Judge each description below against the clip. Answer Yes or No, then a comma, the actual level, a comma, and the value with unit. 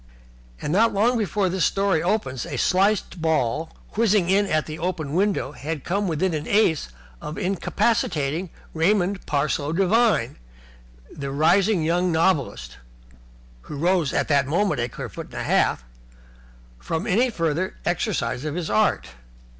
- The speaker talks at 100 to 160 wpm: Yes, average, 145 wpm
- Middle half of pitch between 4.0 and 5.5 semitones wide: Yes, average, 4.7 semitones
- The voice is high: No, medium, 170 Hz